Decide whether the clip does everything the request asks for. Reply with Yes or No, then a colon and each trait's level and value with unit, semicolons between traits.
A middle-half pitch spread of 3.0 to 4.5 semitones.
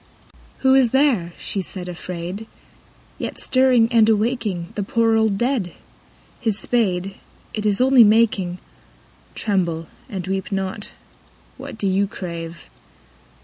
Yes: average, 4.0 semitones